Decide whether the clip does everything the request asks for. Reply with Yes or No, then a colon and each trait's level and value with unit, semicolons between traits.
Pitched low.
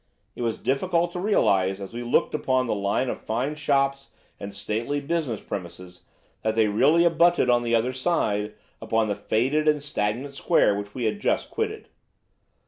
Yes: low, 125 Hz